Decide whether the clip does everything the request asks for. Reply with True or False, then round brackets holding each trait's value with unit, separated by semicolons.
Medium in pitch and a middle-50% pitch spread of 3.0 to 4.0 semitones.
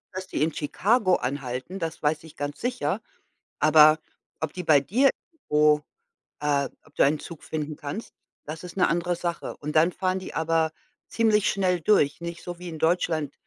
True (160 Hz; 3.4 semitones)